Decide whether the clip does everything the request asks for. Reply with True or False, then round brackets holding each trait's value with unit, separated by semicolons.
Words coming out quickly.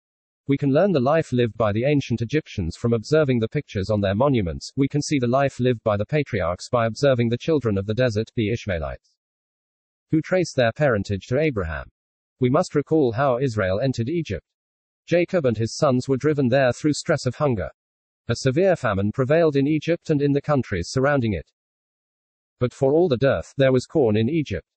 False (195 wpm)